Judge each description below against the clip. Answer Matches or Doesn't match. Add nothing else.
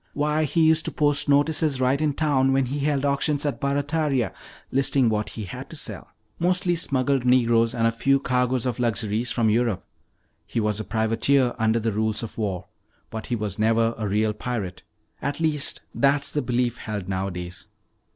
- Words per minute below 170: Doesn't match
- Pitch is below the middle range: Matches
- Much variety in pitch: Doesn't match